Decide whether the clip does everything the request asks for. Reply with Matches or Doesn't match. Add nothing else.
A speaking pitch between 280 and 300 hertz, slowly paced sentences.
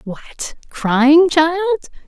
Matches